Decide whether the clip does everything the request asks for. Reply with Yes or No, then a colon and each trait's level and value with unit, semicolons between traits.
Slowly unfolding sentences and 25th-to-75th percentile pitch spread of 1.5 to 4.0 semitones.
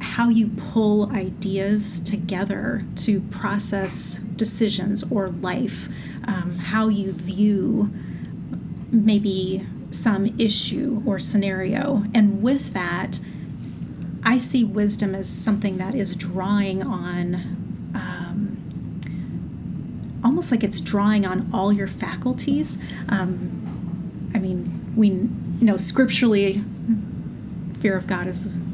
Yes: slow, 105 wpm; narrow, 2.5 semitones